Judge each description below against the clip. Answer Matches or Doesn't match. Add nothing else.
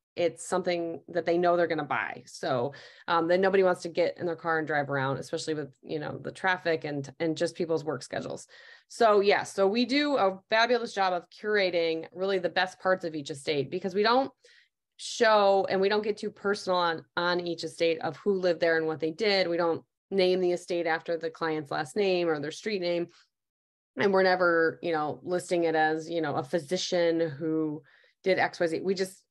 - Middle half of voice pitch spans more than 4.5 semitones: Doesn't match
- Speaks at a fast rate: Matches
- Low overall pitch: Doesn't match